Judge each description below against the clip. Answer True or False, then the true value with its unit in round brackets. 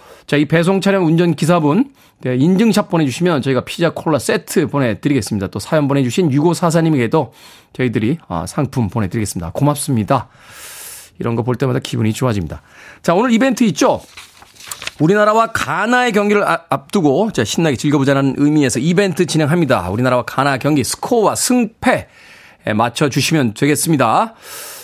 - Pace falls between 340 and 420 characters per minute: True (360 characters per minute)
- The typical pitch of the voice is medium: True (145 Hz)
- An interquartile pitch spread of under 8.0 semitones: True (5.6 semitones)